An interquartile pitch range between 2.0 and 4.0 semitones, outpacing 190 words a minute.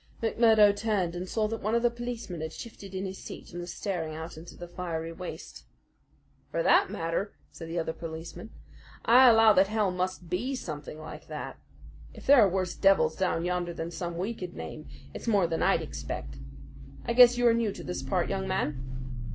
No: average, 4.7 semitones; average, 200 wpm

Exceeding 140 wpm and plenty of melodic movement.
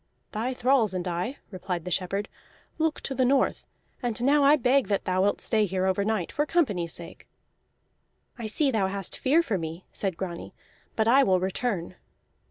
Yes: average, 180 wpm; wide, 5.9 semitones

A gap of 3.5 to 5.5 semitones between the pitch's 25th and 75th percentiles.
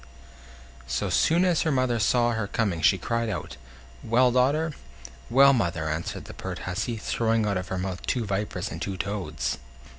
Yes: average, 5.0 semitones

